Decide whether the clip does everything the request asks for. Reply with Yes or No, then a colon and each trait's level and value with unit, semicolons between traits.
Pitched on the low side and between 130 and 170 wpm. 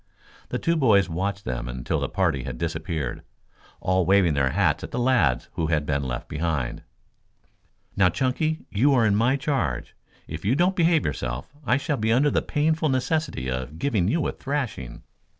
No: very low, 95 Hz; average, 180 wpm